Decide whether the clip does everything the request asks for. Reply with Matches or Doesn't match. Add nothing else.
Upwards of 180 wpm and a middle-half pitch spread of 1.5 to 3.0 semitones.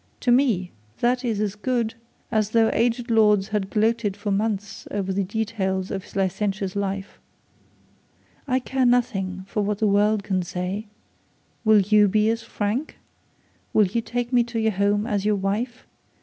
Doesn't match